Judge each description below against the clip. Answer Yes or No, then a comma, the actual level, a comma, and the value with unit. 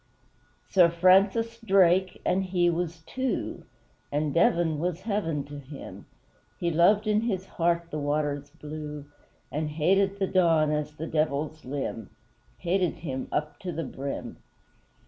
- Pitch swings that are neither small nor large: Yes, average, 3.8 semitones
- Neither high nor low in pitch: Yes, medium, 165 Hz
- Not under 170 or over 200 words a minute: No, average, 140 wpm